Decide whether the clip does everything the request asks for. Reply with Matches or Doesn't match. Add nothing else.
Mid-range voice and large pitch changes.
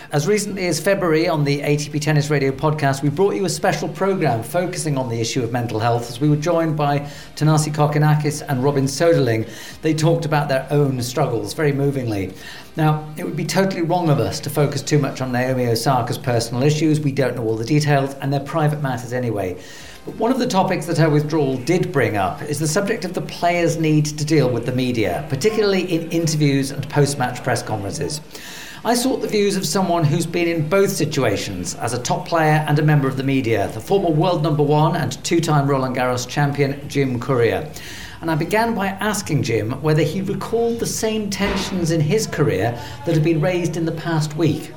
Doesn't match